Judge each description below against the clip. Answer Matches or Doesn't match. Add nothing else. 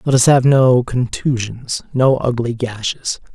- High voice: Doesn't match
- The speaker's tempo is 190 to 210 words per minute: Doesn't match